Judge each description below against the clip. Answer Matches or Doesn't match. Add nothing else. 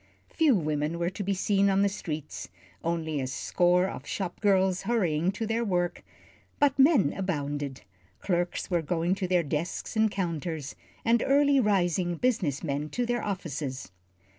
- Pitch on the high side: Doesn't match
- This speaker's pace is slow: Doesn't match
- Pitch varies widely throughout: Doesn't match